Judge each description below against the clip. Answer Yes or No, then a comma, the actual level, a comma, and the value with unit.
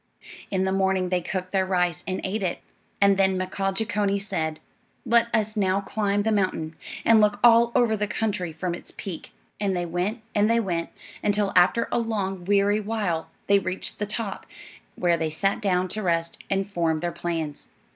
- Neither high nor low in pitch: No, high, 195 Hz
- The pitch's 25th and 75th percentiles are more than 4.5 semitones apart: No, average, 2.8 semitones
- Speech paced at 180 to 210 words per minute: Yes, average, 185 wpm